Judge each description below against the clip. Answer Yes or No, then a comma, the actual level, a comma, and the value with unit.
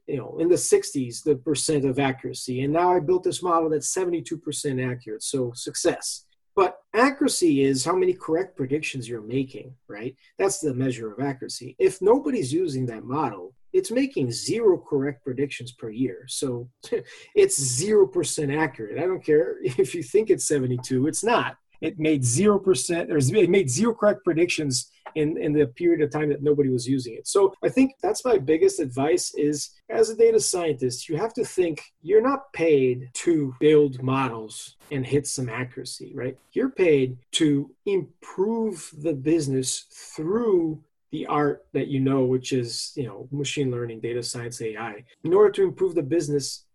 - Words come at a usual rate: Yes, average, 175 wpm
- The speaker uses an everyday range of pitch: No, wide, 7.1 semitones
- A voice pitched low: No, medium, 150 Hz